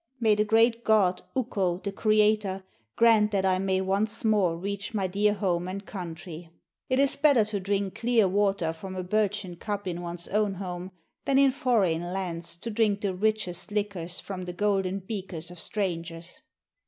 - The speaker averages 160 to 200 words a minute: Yes, average, 175 wpm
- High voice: Yes, high, 195 Hz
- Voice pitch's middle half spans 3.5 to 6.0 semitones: No, average, 2.9 semitones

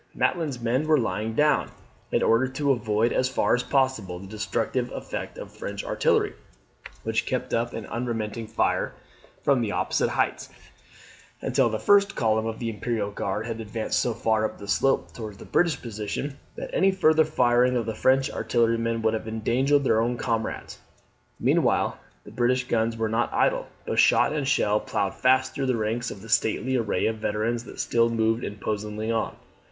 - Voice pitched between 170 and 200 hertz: No, low, 115 Hz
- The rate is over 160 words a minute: Yes, average, 180 wpm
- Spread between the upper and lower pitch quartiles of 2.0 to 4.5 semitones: Yes, average, 2.9 semitones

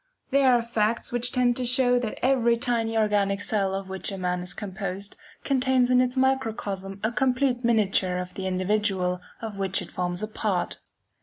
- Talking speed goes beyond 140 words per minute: Yes, average, 180 wpm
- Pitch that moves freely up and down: No, average, 4.3 semitones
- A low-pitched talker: No, high, 215 Hz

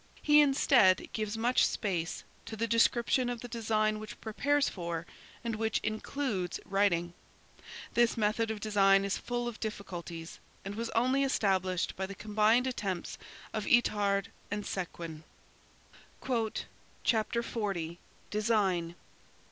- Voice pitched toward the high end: Yes, high, 215 Hz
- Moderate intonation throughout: Yes, average, 3.1 semitones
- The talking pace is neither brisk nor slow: No, slow, 125 wpm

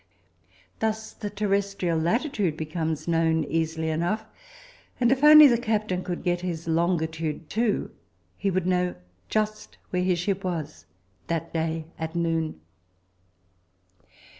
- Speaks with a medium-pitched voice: Yes, medium, 175 Hz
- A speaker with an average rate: No, slow, 125 wpm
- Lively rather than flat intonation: No, average, 4.2 semitones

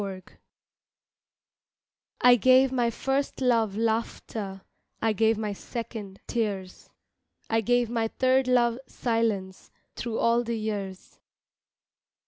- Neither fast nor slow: No, slow, 110 wpm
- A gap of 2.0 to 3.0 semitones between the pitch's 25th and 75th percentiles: Yes, average, 2.7 semitones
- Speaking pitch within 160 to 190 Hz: No, high, 225 Hz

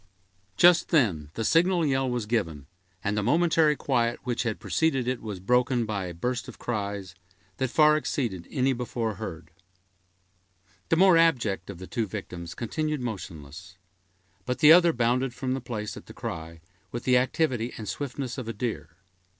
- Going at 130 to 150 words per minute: No, average, 170 wpm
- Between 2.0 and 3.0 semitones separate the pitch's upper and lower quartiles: No, average, 4.9 semitones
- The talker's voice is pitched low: Yes, low, 120 Hz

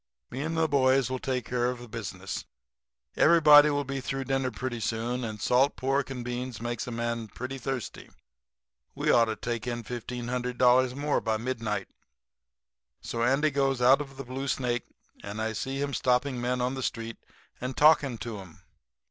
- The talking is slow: No, average, 180 wpm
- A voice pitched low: Yes, low, 125 Hz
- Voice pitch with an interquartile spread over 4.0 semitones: No, narrow, 2.4 semitones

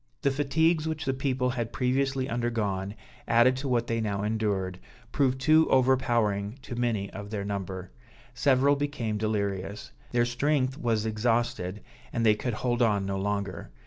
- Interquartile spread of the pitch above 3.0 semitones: Yes, average, 4.3 semitones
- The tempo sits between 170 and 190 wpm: No, average, 155 wpm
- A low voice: Yes, low, 120 Hz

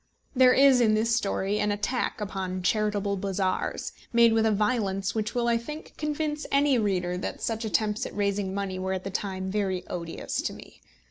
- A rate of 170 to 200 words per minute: Yes, average, 190 wpm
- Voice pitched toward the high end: Yes, high, 210 Hz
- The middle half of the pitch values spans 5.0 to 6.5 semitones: No, average, 3.4 semitones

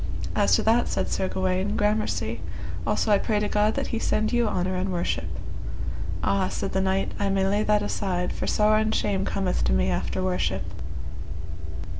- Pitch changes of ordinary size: No, narrow, 2.3 semitones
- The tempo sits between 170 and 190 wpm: Yes, average, 185 wpm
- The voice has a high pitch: Yes, high, 195 Hz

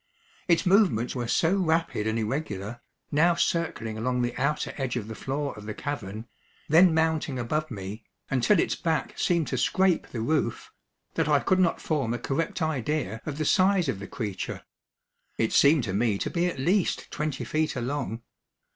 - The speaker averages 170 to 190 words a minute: Yes, average, 180 wpm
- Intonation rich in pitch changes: Yes, wide, 5.9 semitones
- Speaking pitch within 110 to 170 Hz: Yes, medium, 140 Hz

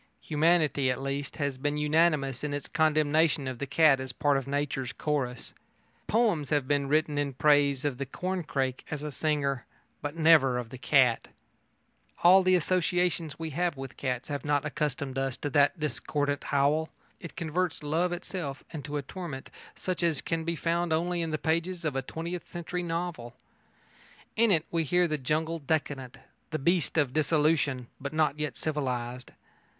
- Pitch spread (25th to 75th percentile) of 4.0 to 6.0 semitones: No, average, 3.2 semitones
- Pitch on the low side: No, medium, 150 Hz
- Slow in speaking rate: No, average, 170 wpm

